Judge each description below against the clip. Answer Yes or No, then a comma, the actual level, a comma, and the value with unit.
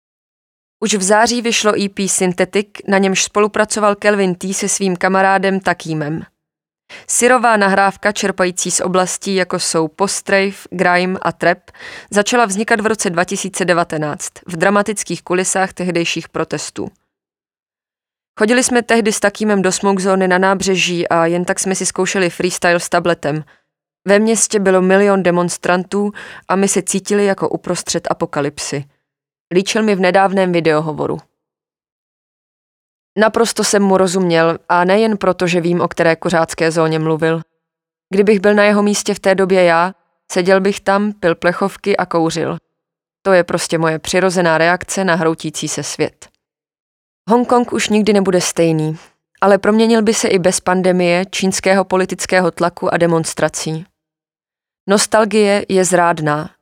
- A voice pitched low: No, medium, 185 Hz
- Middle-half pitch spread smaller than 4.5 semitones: Yes, average, 2.8 semitones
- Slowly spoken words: No, average, 140 wpm